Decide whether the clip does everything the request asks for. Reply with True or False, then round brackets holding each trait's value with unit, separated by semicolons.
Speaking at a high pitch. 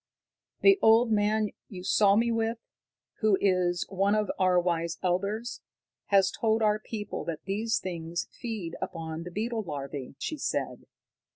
True (200 Hz)